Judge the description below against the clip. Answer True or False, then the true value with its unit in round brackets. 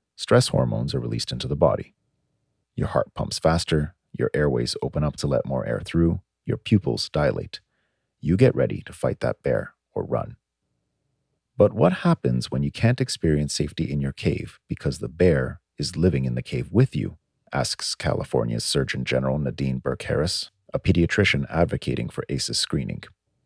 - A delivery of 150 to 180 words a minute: True (170 wpm)